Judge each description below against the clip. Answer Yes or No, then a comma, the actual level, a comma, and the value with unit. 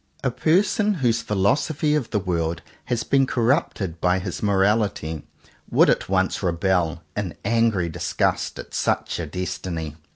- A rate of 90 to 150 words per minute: Yes, average, 140 wpm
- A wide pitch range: Yes, wide, 6.1 semitones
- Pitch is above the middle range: No, low, 100 Hz